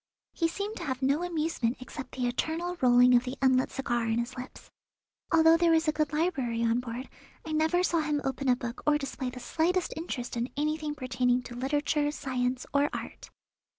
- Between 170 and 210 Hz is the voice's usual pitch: No, very high, 270 Hz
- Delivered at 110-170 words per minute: No, average, 195 wpm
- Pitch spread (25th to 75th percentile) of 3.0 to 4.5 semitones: Yes, average, 4.2 semitones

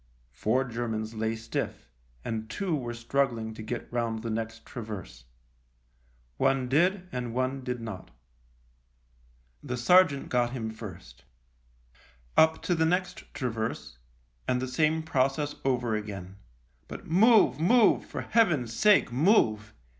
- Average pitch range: Yes, average, 4.8 semitones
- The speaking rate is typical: No, slow, 130 wpm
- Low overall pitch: Yes, low, 125 Hz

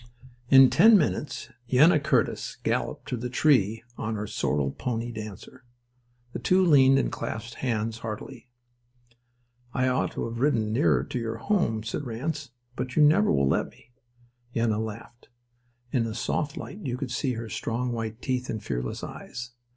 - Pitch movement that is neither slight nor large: Yes, average, 3.4 semitones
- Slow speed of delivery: No, average, 165 wpm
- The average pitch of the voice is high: No, low, 120 Hz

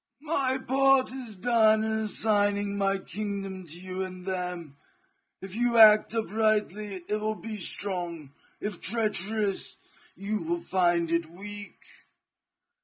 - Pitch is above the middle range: Yes, high, 205 Hz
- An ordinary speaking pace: No, slow, 125 wpm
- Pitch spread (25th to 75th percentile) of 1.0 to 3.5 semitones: Yes, average, 2.8 semitones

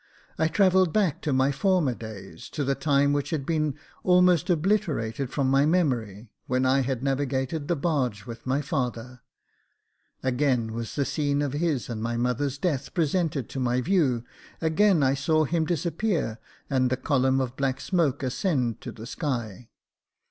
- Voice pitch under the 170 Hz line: Yes, medium, 140 Hz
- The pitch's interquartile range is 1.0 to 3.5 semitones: No, average, 4.1 semitones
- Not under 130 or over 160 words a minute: No, average, 170 wpm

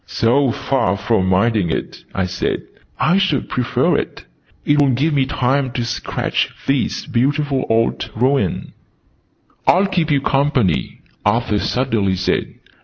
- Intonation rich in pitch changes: No, average, 4.8 semitones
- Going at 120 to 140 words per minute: Yes, slow, 135 wpm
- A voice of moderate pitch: No, low, 125 Hz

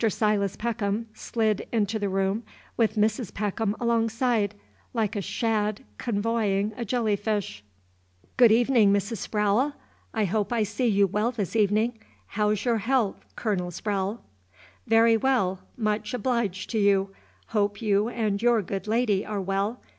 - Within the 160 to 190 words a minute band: No, average, 145 wpm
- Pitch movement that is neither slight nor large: No, narrow, 2.3 semitones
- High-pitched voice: Yes, high, 215 Hz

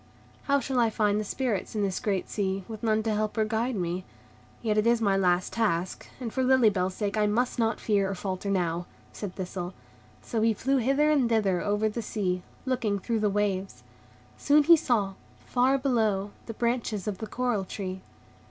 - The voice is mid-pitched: No, high, 215 Hz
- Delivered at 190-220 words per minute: Yes, average, 200 wpm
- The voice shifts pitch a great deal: No, average, 3.4 semitones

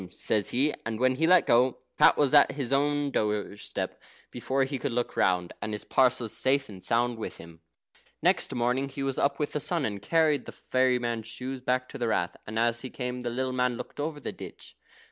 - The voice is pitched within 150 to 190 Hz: No, low, 125 Hz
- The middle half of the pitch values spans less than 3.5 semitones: Yes, average, 3.0 semitones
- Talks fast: Yes, fast, 220 wpm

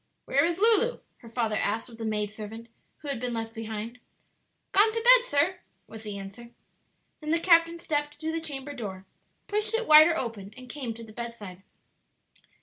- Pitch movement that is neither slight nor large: No, wide, 6.7 semitones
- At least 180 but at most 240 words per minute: Yes, average, 185 wpm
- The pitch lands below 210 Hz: No, very high, 250 Hz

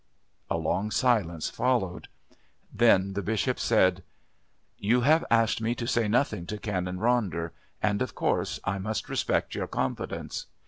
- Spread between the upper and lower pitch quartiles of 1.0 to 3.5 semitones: No, average, 4.2 semitones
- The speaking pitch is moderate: No, low, 105 Hz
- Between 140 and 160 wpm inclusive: Yes, average, 145 wpm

